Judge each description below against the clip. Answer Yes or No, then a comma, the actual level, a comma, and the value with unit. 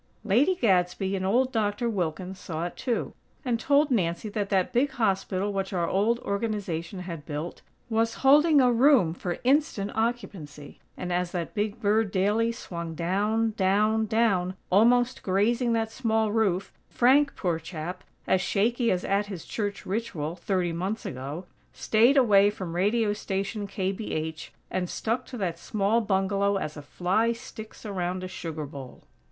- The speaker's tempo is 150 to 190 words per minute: Yes, average, 160 wpm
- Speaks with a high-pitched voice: Yes, high, 200 Hz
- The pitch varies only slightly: No, average, 4.0 semitones